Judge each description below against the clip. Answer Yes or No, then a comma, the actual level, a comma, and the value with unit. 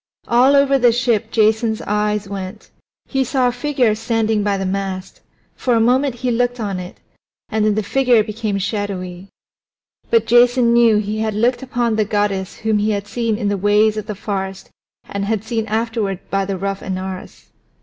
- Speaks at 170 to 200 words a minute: Yes, average, 190 wpm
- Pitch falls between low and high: No, high, 215 Hz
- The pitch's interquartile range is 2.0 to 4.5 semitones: Yes, average, 2.9 semitones